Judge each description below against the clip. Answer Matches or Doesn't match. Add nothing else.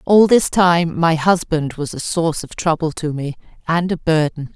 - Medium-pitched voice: Matches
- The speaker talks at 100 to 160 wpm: Doesn't match